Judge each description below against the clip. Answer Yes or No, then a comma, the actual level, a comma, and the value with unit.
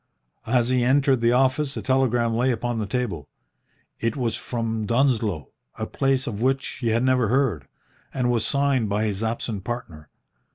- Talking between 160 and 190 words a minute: Yes, average, 170 wpm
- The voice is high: No, low, 120 Hz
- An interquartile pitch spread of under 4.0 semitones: Yes, average, 2.7 semitones